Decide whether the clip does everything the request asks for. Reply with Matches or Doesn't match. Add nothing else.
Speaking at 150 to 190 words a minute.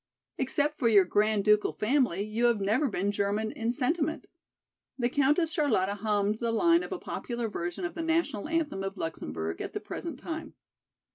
Matches